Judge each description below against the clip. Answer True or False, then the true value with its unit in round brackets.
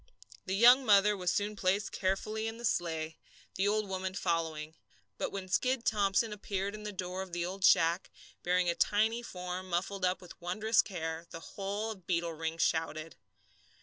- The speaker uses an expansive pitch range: False (3.2 semitones)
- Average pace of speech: True (180 wpm)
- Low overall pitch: False (190 Hz)